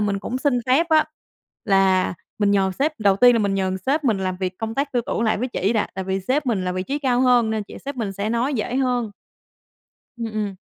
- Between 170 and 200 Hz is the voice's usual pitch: No, high, 220 Hz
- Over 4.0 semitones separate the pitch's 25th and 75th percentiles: Yes, average, 4.7 semitones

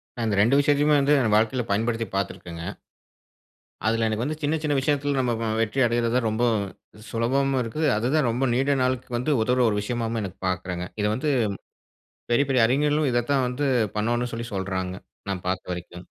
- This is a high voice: No, low, 120 Hz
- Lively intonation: No, average, 4.1 semitones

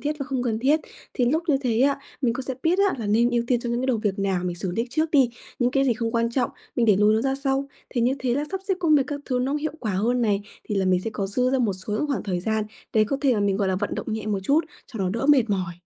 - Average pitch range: Yes, average, 4.6 semitones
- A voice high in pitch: Yes, high, 240 Hz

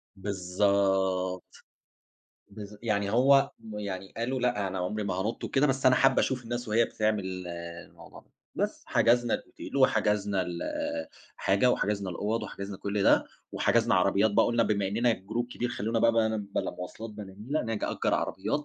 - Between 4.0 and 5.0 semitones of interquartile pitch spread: No, average, 3.2 semitones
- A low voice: Yes, low, 105 Hz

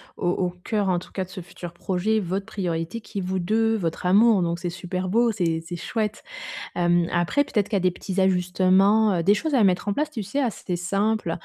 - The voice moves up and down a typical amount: Yes, average, 3.3 semitones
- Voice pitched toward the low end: No, high, 190 Hz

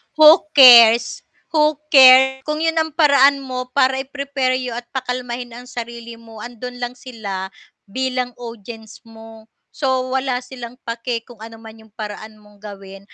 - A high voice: Yes, high, 245 Hz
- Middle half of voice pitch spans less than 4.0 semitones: Yes, average, 2.7 semitones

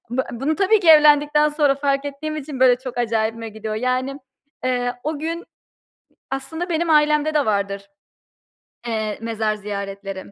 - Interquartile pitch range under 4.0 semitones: No, wide, 5.4 semitones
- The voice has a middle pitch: No, very high, 265 Hz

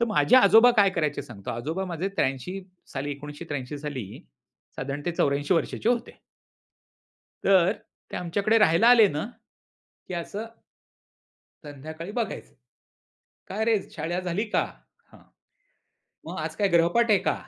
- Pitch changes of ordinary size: No, wide, 5.9 semitones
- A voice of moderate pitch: Yes, medium, 170 Hz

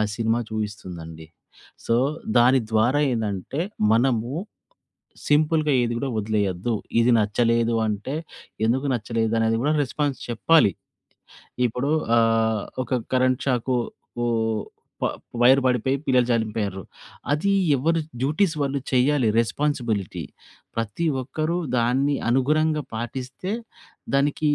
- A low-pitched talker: Yes, low, 120 Hz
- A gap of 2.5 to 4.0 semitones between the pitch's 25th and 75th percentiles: Yes, average, 3.7 semitones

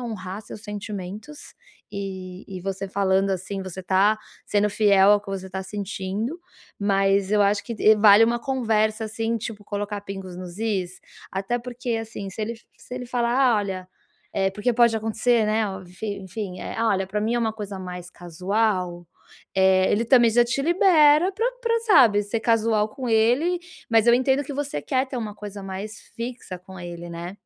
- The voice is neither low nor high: No, high, 210 Hz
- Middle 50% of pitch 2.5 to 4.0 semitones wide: Yes, average, 3.4 semitones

